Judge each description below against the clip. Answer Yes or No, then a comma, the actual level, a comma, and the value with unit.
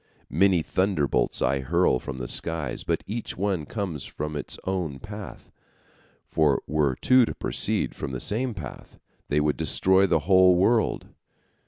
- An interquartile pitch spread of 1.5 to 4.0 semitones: No, average, 5.2 semitones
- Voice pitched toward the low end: Yes, very low, 85 Hz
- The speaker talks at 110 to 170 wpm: Yes, average, 155 wpm